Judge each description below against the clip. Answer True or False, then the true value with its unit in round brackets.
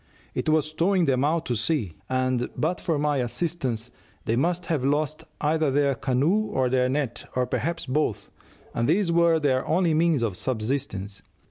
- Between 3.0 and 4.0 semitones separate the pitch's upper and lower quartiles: False (4.4 semitones)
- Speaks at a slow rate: False (170 wpm)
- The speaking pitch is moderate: True (145 Hz)